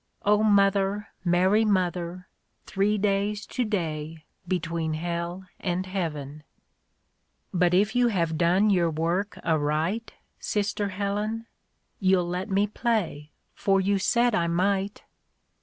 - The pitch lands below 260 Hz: Yes, high, 190 Hz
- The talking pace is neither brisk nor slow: No, slow, 120 wpm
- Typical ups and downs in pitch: Yes, average, 3.2 semitones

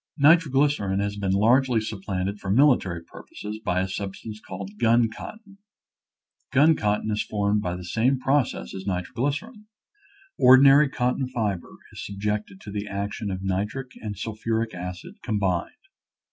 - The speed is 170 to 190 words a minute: No, average, 145 wpm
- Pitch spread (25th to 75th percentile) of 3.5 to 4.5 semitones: No, average, 4.9 semitones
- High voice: No, low, 105 Hz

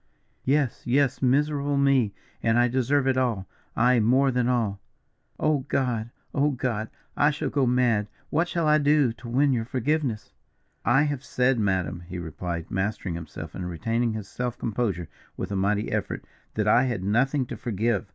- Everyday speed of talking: Yes, average, 170 wpm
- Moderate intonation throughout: Yes, average, 4.5 semitones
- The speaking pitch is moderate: No, low, 120 Hz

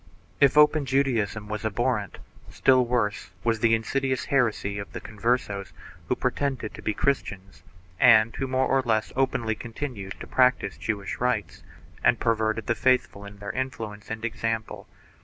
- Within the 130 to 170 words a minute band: Yes, average, 160 wpm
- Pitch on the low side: Yes, low, 115 Hz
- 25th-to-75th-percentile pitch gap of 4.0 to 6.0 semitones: No, average, 3.5 semitones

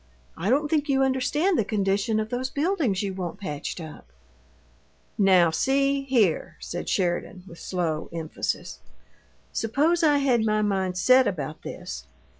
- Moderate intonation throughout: No, wide, 7.1 semitones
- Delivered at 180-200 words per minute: No, average, 145 wpm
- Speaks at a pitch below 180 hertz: No, high, 215 Hz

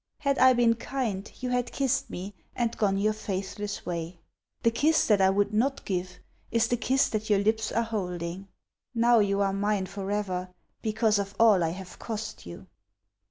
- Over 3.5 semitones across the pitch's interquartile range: No, average, 3.1 semitones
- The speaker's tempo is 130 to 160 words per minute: No, average, 180 wpm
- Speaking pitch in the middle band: No, high, 210 Hz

